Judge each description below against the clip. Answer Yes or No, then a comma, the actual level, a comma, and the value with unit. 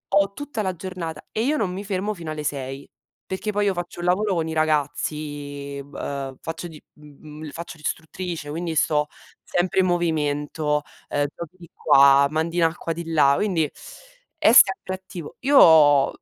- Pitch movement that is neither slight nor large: Yes, average, 4.1 semitones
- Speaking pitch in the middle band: Yes, medium, 165 Hz